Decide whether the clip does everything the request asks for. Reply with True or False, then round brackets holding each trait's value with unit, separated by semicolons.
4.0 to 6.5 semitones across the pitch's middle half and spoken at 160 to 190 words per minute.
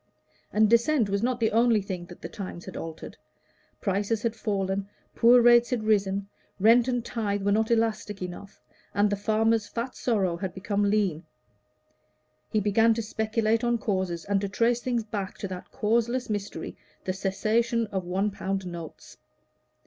False (3.0 semitones; 165 wpm)